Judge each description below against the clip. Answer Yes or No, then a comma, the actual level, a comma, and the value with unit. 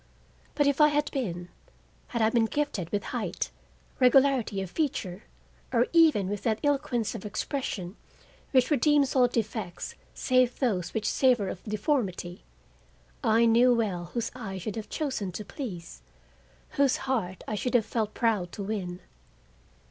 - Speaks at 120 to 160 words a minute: Yes, average, 155 wpm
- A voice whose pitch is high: Yes, high, 225 Hz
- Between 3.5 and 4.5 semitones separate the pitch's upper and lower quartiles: No, average, 5.0 semitones